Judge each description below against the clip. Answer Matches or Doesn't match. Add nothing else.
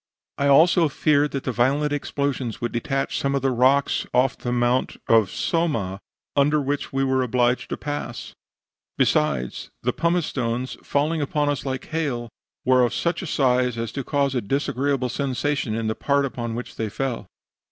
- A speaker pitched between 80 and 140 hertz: Matches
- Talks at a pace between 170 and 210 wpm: Matches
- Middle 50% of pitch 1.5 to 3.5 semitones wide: Matches